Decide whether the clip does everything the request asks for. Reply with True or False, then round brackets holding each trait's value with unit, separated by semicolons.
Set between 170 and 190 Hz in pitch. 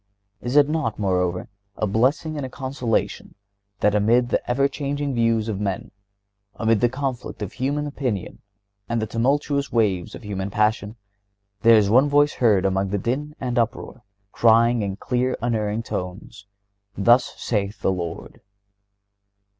False (115 Hz)